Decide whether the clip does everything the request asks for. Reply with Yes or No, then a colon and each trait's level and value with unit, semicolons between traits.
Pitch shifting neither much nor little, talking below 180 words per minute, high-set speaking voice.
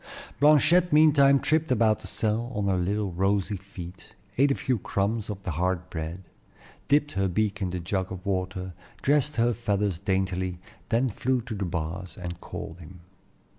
No: average, 4.6 semitones; average, 170 wpm; low, 100 Hz